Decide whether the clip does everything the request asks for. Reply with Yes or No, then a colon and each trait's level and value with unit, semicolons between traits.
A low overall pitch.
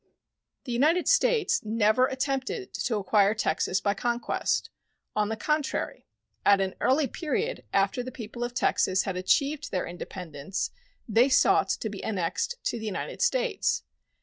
No: high, 230 Hz